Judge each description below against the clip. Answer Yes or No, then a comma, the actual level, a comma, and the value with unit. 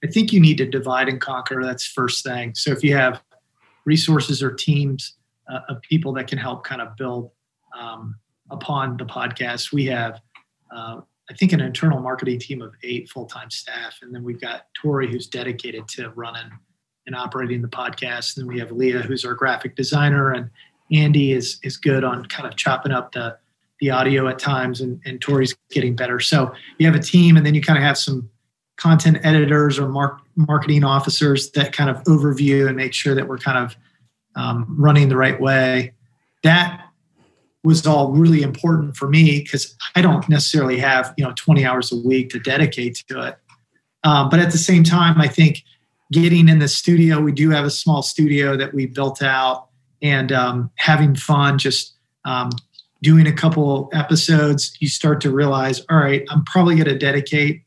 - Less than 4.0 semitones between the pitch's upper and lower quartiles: Yes, average, 3.1 semitones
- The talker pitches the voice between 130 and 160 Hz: Yes, low, 135 Hz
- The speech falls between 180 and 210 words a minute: Yes, average, 195 wpm